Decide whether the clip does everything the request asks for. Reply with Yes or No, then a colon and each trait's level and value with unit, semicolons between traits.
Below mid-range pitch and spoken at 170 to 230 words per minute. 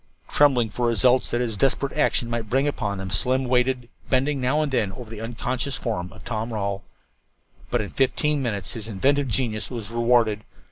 Yes: low, 120 Hz; average, 195 wpm